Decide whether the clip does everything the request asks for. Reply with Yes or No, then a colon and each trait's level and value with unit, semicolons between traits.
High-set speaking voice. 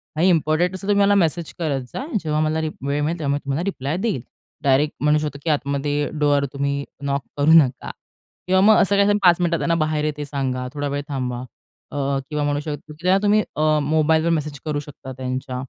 No: medium, 150 Hz